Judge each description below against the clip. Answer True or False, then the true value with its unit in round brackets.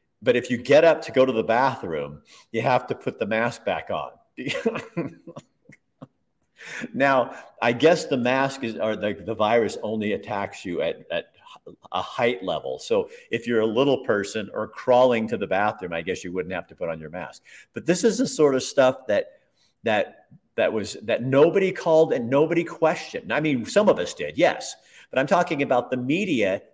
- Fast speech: False (195 wpm)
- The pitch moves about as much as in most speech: False (7.3 semitones)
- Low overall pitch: True (130 Hz)